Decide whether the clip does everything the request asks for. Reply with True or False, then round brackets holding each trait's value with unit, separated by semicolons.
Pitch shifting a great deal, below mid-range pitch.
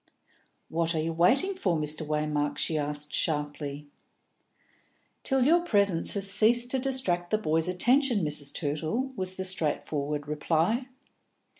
False (6.5 semitones; 170 Hz)